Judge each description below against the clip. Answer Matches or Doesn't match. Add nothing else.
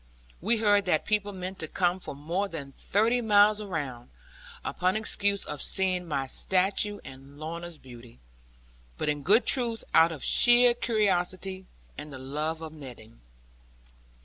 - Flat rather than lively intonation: Doesn't match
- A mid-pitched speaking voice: Matches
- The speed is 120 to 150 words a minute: Matches